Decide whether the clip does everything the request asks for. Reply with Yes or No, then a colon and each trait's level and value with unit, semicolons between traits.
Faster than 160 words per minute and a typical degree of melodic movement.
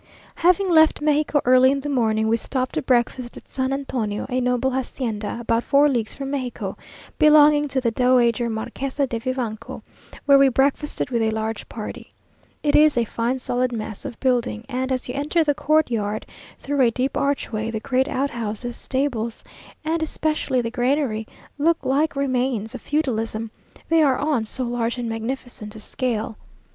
Yes: average, 170 wpm; average, 3.5 semitones